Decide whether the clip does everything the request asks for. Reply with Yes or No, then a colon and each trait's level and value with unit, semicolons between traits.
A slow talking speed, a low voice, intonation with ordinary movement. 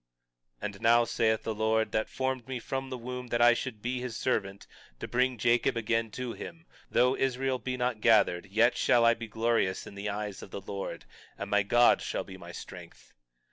No: average, 200 wpm; low, 115 Hz; average, 3.0 semitones